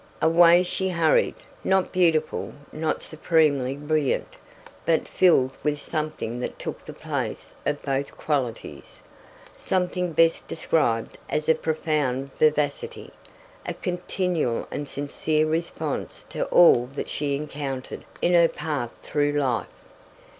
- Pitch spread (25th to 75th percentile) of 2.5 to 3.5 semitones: Yes, average, 3.0 semitones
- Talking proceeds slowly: Yes, slow, 120 wpm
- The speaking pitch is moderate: Yes, medium, 155 Hz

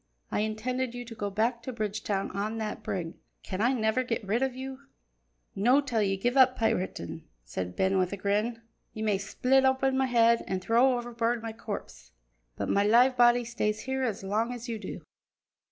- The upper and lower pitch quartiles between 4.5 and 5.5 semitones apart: No, average, 3.2 semitones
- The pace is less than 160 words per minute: No, average, 195 wpm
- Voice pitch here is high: Yes, high, 230 Hz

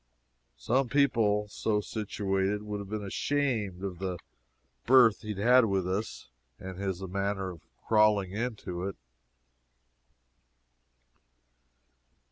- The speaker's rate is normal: No, slow, 105 wpm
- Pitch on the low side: Yes, low, 105 Hz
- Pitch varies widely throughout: No, narrow, 2.5 semitones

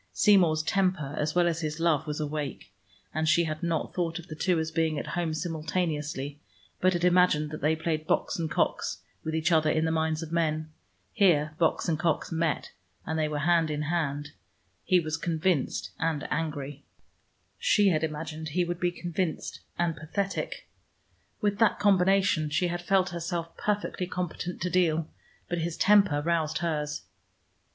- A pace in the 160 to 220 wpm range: Yes, average, 170 wpm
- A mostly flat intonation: Yes, narrow, 2.2 semitones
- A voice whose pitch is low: No, medium, 165 Hz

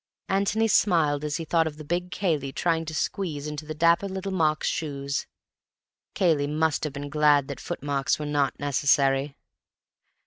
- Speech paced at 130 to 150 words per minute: No, average, 165 wpm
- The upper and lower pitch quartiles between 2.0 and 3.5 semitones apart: Yes, average, 2.8 semitones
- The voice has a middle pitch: Yes, medium, 150 Hz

